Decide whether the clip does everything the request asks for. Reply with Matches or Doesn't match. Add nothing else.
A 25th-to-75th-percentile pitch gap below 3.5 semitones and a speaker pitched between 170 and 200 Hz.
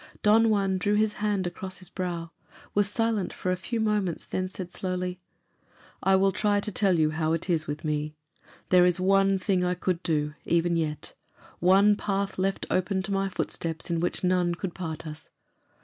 Matches